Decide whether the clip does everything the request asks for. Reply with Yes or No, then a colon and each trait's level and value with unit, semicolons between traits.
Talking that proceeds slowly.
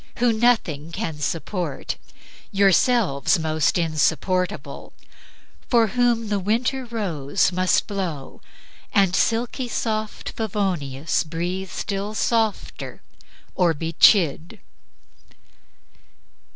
Yes: slow, 85 wpm